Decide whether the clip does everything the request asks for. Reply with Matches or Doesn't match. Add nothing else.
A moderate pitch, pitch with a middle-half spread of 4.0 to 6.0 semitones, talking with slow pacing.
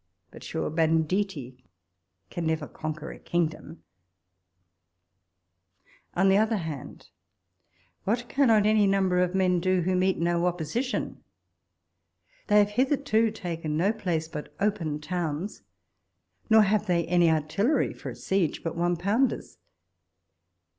Matches